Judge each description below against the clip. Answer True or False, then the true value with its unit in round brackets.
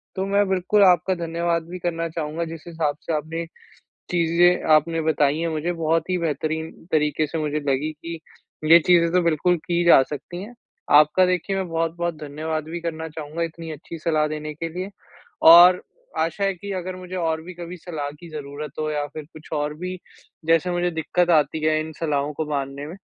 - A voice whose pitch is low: False (165 Hz)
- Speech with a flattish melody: True (2.3 semitones)